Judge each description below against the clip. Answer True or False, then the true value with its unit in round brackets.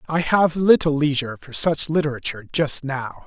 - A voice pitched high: False (150 Hz)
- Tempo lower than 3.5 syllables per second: False (5.3 syllables/s)